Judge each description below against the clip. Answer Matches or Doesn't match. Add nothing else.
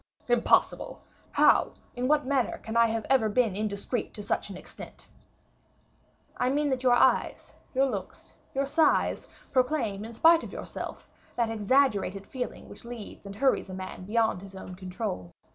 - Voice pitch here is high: Matches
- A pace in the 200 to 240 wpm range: Doesn't match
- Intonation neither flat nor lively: Matches